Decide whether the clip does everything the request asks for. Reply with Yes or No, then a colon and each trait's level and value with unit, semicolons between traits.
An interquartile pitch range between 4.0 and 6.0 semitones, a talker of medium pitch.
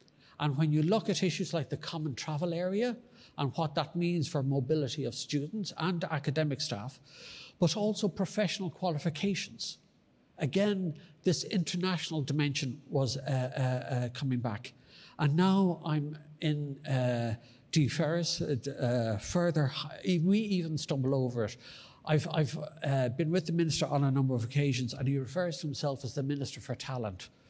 Yes: average, 4.3 semitones; medium, 150 Hz